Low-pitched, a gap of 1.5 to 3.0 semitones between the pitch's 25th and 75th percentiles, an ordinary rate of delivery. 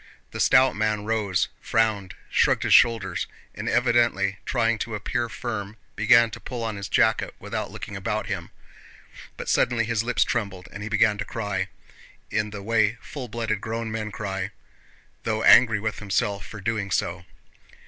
Yes: low, 110 Hz; narrow, 2.4 semitones; average, 170 wpm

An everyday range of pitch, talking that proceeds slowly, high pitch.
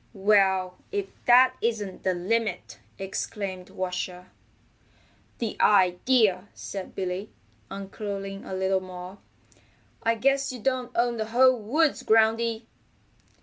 Yes: average, 3.9 semitones; slow, 110 wpm; high, 205 Hz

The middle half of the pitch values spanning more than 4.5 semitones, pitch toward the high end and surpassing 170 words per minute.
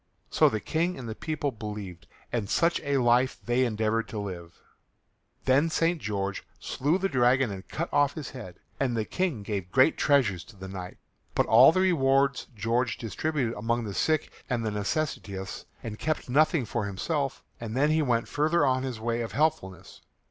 No: wide, 5.4 semitones; low, 120 Hz; average, 180 wpm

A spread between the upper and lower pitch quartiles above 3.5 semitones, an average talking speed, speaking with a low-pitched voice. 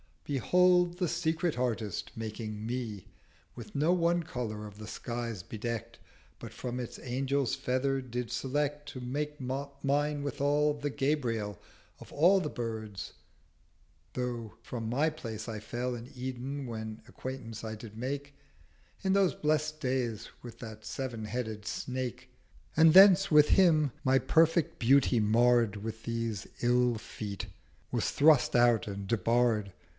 Yes: average, 4.5 semitones; average, 145 wpm; low, 125 Hz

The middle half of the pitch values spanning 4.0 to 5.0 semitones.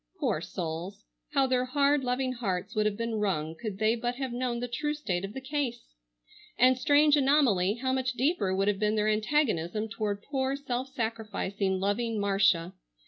Yes: average, 4.6 semitones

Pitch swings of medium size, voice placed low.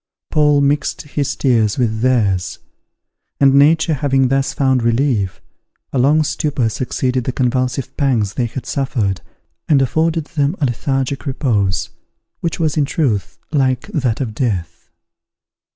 Yes: average, 3.5 semitones; low, 130 Hz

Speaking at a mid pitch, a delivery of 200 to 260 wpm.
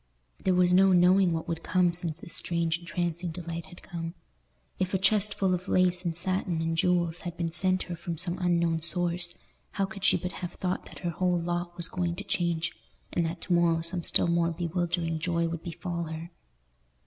Yes: medium, 175 Hz; fast, 205 wpm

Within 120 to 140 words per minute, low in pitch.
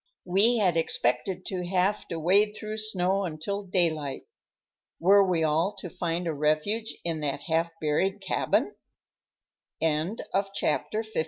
No: slow, 135 wpm; medium, 180 Hz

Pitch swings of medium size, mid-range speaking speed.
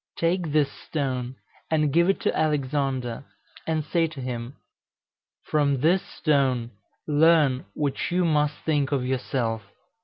No: average, 3.4 semitones; slow, 130 wpm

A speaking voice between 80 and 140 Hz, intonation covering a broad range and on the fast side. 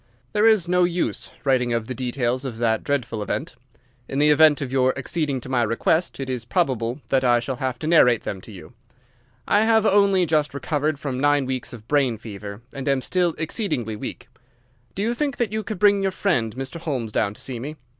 Yes: low, 135 Hz; wide, 6.0 semitones; fast, 215 wpm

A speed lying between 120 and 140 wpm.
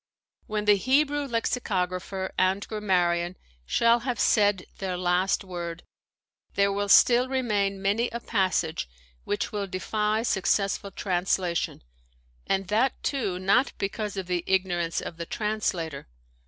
Yes: slow, 135 wpm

